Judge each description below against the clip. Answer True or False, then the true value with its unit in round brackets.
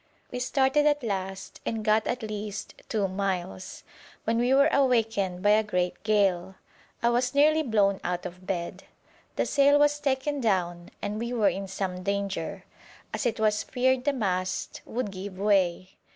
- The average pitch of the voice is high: True (210 Hz)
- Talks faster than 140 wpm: True (165 wpm)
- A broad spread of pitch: False (4.8 semitones)